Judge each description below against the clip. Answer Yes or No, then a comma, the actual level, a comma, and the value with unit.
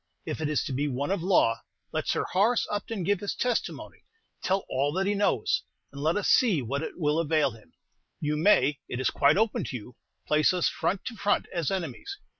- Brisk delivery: Yes, fast, 215 wpm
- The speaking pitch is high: No, medium, 165 Hz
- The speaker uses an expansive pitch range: Yes, wide, 6.0 semitones